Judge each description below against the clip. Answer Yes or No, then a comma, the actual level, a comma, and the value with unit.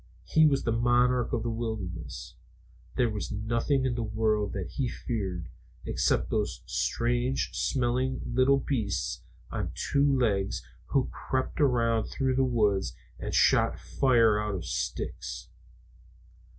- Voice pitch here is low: Yes, low, 120 Hz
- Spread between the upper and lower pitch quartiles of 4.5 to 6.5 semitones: No, average, 3.5 semitones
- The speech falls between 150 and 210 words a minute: No, slow, 135 wpm